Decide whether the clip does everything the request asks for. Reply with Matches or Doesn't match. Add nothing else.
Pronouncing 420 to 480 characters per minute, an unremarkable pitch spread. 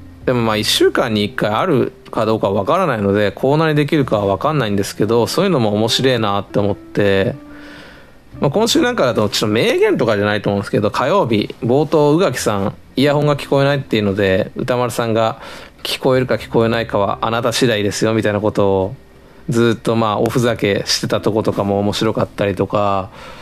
Matches